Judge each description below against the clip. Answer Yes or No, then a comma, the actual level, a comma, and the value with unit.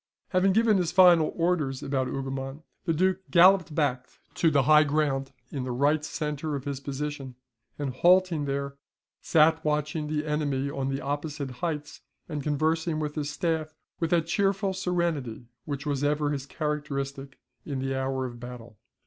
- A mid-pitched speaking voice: Yes, medium, 150 Hz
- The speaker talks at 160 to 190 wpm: Yes, average, 165 wpm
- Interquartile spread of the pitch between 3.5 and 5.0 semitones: No, average, 3.0 semitones